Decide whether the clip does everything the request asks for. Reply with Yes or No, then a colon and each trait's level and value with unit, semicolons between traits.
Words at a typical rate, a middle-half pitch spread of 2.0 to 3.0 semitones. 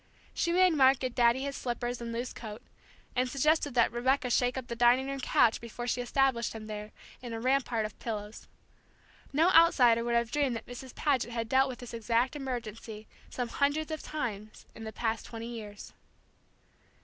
Yes: average, 185 wpm; average, 2.7 semitones